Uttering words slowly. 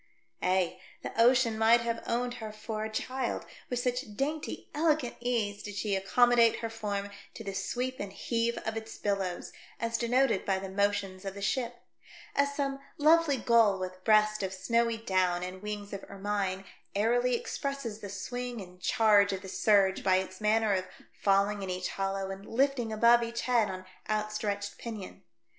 No: average, 175 wpm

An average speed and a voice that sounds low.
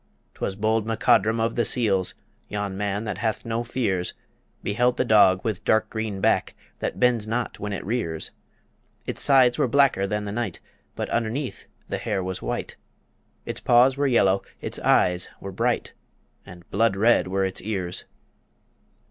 Yes: average, 165 wpm; low, 110 Hz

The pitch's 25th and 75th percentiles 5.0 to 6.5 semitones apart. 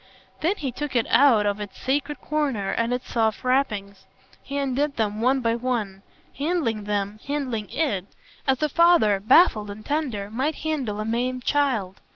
Yes: average, 5.3 semitones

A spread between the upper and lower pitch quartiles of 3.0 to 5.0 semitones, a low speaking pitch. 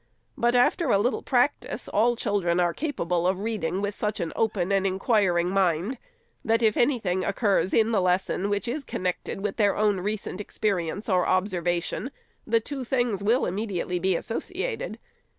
No: average, 3.9 semitones; high, 205 Hz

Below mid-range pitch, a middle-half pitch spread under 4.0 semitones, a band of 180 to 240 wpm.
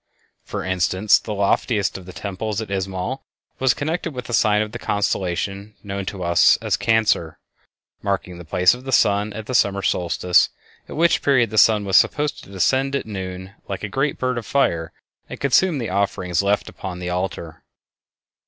No: low, 100 Hz; average, 4.3 semitones; average, 185 wpm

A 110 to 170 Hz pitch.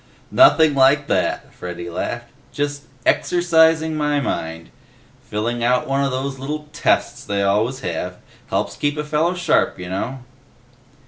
Yes: low, 135 Hz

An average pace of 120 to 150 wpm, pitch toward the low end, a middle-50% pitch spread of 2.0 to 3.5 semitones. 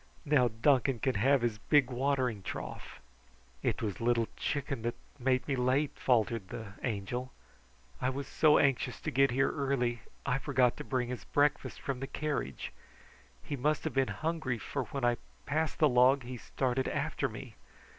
No: average, 170 wpm; low, 130 Hz; narrow, 2.6 semitones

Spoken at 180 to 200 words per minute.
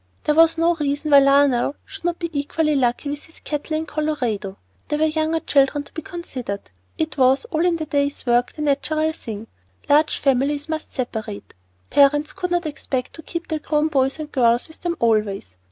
Yes: average, 195 wpm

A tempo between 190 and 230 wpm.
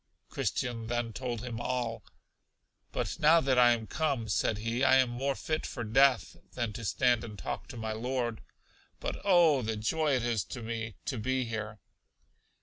No: average, 180 wpm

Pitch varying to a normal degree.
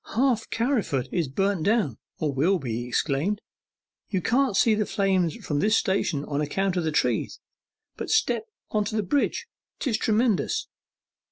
No: wide, 6.5 semitones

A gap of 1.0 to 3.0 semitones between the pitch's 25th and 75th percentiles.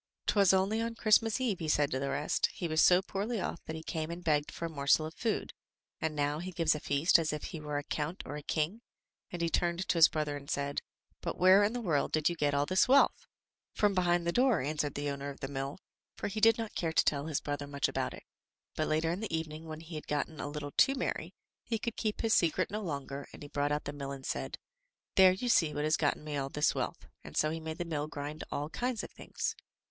No: average, 4.2 semitones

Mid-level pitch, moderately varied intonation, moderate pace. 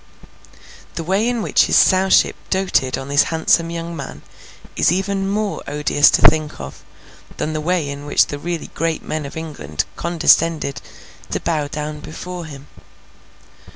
Yes: medium, 160 Hz; average, 3.4 semitones; average, 155 wpm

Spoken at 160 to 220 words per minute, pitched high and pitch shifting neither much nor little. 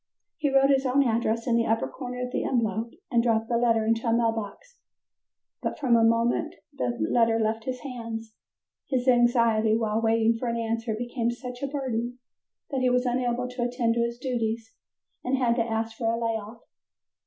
No: average, 200 wpm; high, 235 Hz; narrow, 1.7 semitones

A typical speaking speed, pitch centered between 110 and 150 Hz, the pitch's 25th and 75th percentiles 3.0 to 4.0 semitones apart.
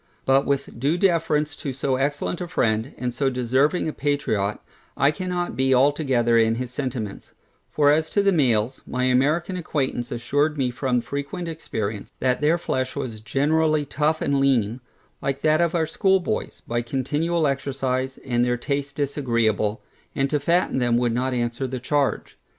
Yes: average, 165 wpm; low, 135 Hz; average, 3.6 semitones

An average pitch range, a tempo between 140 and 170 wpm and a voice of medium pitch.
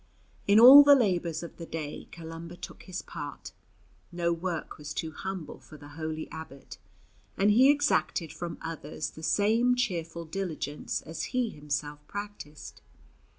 Yes: average, 4.4 semitones; average, 150 wpm; medium, 170 Hz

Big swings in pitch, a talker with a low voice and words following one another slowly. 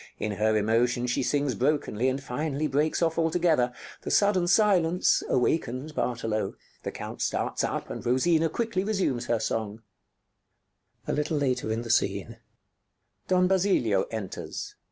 Yes: wide, 6.2 semitones; low, 130 Hz; slow, 115 wpm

